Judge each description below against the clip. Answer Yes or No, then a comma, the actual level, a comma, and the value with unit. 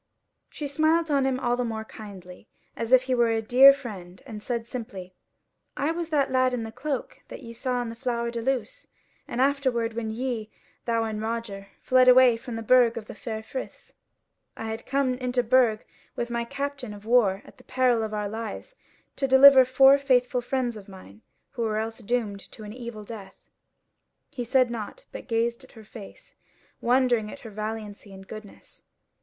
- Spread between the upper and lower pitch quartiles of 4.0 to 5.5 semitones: No, average, 2.8 semitones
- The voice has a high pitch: Yes, high, 235 Hz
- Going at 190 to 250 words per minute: Yes, average, 195 wpm